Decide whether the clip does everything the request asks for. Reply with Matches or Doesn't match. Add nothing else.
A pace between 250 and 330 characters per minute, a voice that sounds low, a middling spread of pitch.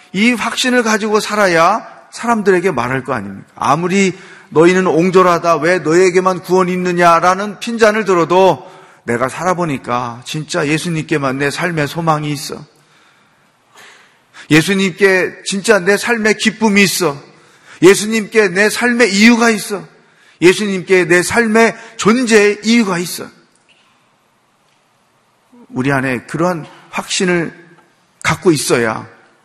Doesn't match